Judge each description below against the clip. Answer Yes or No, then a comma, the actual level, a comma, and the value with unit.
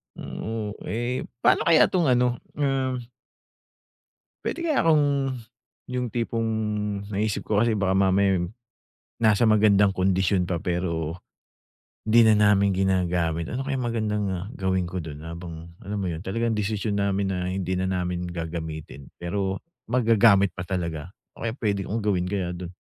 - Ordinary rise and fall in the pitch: Yes, average, 3.9 semitones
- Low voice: Yes, low, 100 Hz